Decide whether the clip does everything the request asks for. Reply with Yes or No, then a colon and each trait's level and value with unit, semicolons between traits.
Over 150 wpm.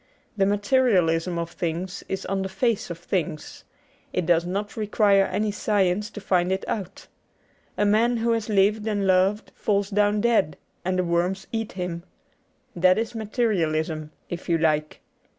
Yes: average, 160 wpm